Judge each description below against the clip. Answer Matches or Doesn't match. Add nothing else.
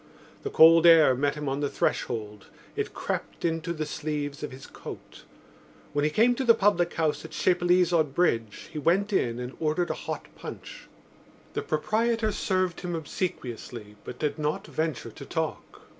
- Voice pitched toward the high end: Doesn't match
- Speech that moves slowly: Doesn't match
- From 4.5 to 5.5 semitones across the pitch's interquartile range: Doesn't match